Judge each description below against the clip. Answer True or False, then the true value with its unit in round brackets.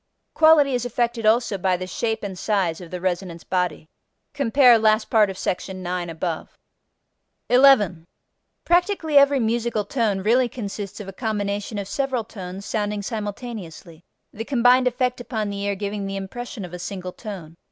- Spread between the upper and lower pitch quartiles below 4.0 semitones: False (4.3 semitones)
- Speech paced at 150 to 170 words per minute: True (165 wpm)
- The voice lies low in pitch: False (210 Hz)